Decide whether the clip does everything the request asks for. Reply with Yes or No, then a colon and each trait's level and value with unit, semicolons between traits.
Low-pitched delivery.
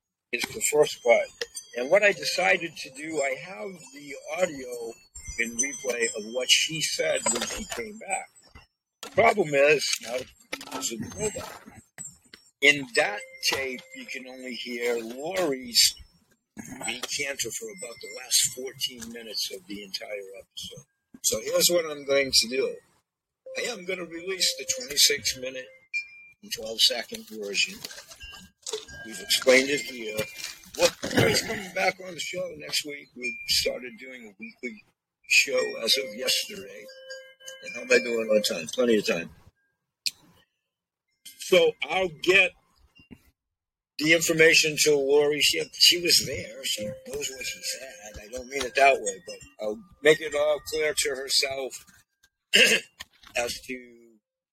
No: medium, 150 Hz